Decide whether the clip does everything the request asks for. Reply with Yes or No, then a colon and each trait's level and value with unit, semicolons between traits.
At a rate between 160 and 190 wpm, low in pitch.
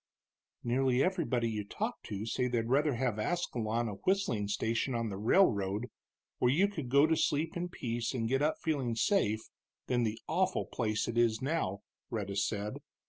Yes: average, 175 wpm; low, 120 Hz